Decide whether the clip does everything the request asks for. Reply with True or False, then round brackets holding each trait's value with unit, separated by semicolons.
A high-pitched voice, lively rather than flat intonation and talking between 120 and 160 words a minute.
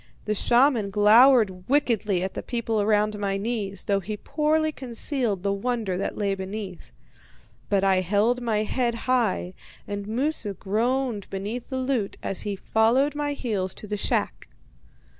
False (215 Hz; 3.8 semitones; 155 wpm)